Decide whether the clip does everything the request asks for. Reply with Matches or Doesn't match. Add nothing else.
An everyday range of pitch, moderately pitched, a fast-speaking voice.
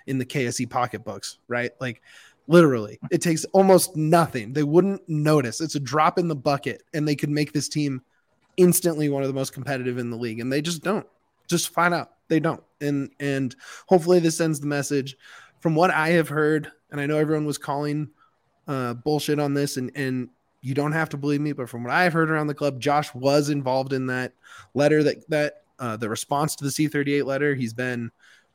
Matches